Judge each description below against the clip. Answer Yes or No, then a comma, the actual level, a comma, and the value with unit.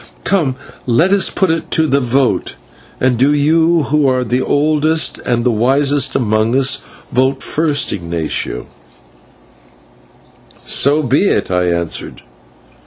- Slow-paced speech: Yes, slow, 130 wpm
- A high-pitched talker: No, low, 135 Hz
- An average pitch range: Yes, average, 4.1 semitones